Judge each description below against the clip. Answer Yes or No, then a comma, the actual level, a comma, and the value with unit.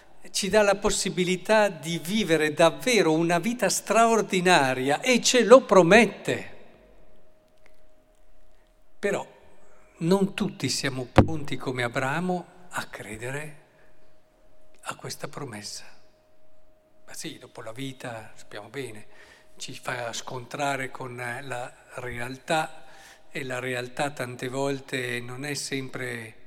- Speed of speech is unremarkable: No, slow, 105 wpm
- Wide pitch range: Yes, wide, 6.4 semitones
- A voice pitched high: No, medium, 145 Hz